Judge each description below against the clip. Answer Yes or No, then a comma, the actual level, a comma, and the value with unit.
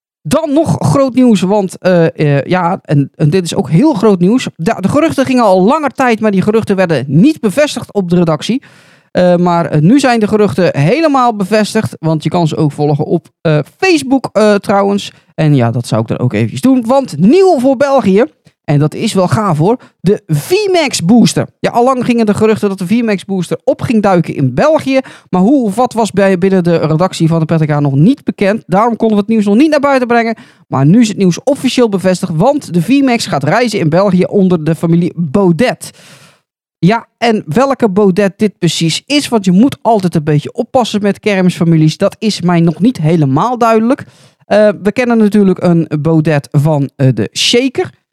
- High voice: Yes, high, 195 Hz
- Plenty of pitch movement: Yes, wide, 6.2 semitones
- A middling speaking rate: No, fast, 205 wpm